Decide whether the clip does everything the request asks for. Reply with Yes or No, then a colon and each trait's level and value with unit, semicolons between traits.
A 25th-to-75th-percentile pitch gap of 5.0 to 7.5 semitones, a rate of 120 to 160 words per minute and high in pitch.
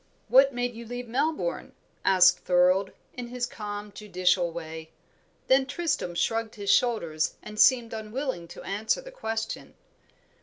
Yes: average, 5.3 semitones; average, 140 wpm; high, 220 Hz